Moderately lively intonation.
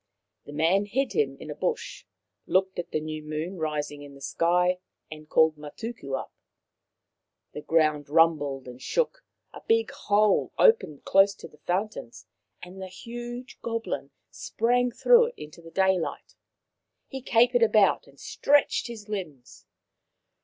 No: wide, 7.2 semitones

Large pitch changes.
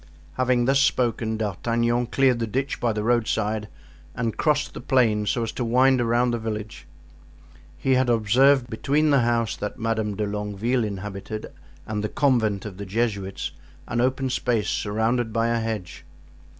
No: average, 2.8 semitones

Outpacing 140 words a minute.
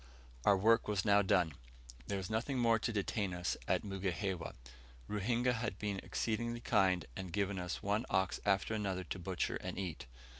Yes: average, 175 wpm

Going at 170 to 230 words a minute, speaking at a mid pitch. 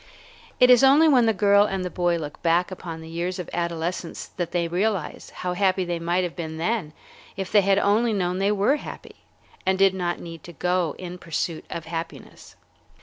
Yes: fast, 205 wpm; medium, 180 Hz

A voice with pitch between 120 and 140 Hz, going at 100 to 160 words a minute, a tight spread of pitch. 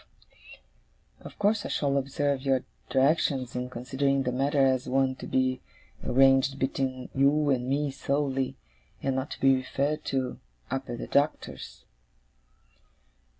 Yes: low, 135 Hz; average, 140 wpm; narrow, 1.3 semitones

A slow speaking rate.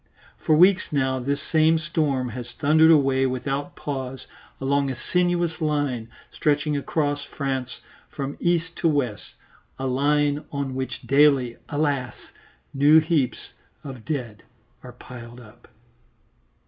Yes: slow, 125 wpm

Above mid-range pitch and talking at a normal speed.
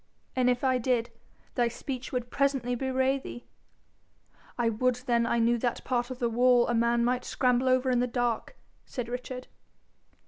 Yes: high, 245 Hz; average, 175 wpm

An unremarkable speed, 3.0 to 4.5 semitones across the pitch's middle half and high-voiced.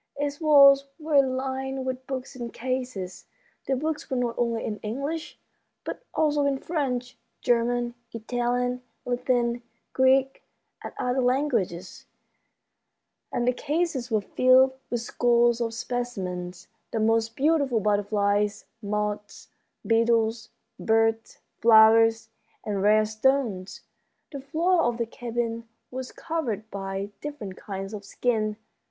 No: slow, 120 wpm; average, 3.3 semitones; high, 240 Hz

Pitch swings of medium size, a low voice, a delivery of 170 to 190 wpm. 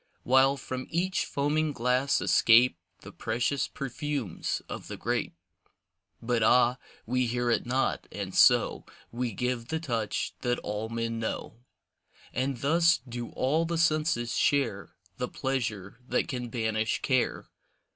No: average, 3.2 semitones; low, 125 Hz; slow, 135 wpm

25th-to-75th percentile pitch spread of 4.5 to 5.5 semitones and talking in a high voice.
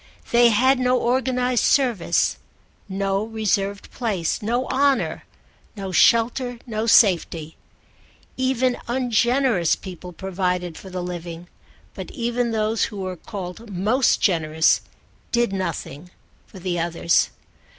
Yes: average, 5.2 semitones; high, 210 Hz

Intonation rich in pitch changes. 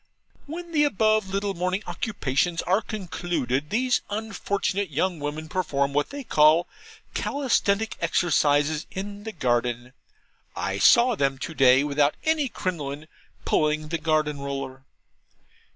Yes: wide, 6.1 semitones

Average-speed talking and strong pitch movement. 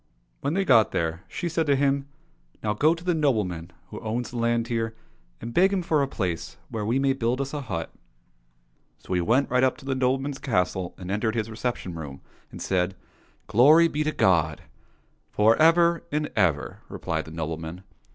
No: fast, 210 wpm; wide, 7.4 semitones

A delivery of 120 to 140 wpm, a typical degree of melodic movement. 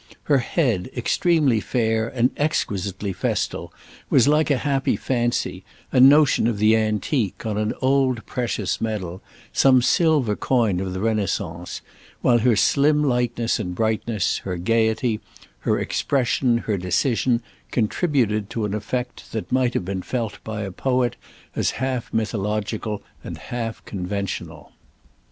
Yes: slow, 135 wpm; average, 3.8 semitones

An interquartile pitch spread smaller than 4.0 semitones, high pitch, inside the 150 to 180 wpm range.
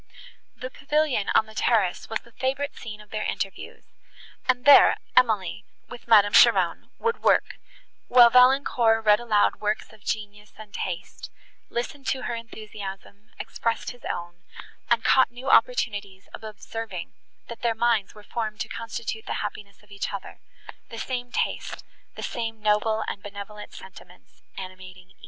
Yes: average, 2.7 semitones; high, 220 Hz; average, 155 wpm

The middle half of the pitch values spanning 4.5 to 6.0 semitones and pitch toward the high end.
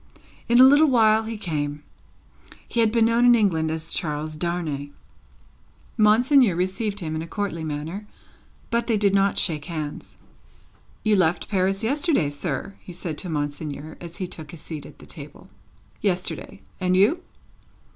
No: wide, 5.5 semitones; medium, 180 Hz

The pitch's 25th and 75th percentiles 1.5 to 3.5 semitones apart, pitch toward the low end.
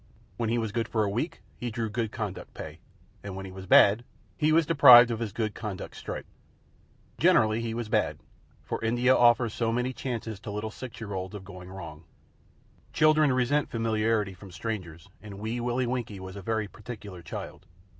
Yes: average, 3.1 semitones; low, 110 Hz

